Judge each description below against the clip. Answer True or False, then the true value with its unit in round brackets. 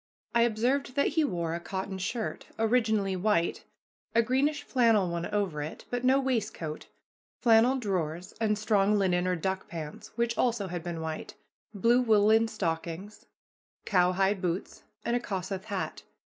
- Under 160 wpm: True (150 wpm)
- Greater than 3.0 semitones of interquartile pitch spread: True (4.5 semitones)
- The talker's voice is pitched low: False (205 Hz)